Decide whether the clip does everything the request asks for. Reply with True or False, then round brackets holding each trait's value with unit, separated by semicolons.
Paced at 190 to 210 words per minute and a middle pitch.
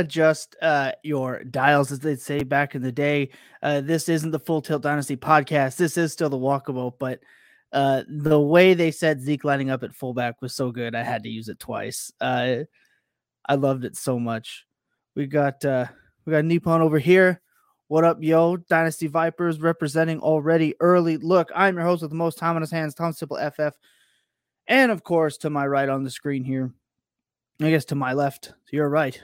True (195 wpm; 150 Hz)